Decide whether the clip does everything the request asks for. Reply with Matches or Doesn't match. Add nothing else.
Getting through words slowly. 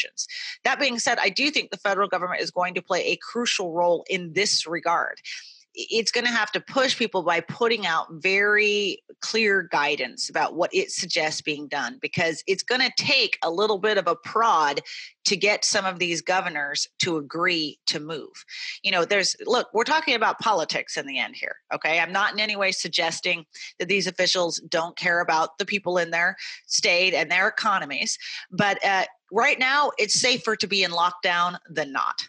Doesn't match